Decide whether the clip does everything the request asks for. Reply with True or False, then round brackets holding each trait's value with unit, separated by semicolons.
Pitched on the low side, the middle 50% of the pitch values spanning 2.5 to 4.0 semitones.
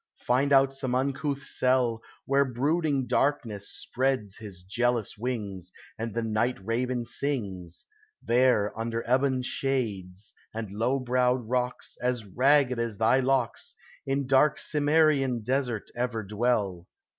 True (125 Hz; 3.3 semitones)